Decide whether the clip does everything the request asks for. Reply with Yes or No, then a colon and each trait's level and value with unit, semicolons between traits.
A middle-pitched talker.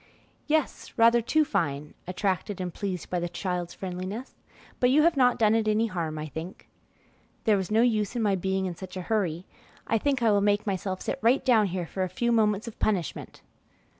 No: high, 205 Hz